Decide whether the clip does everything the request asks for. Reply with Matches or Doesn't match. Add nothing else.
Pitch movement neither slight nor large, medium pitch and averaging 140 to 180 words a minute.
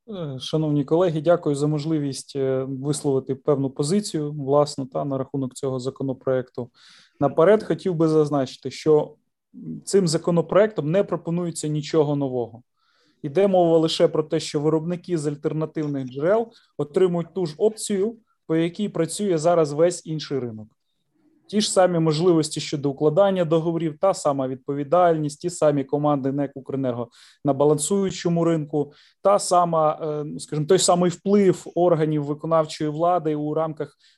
Doesn't match